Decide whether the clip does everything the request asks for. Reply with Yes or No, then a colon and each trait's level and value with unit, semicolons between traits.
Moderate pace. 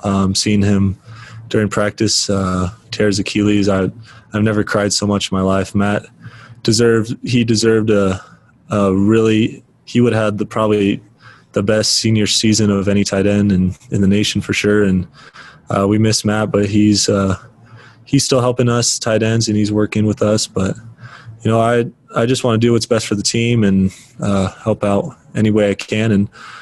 Yes: average, 195 wpm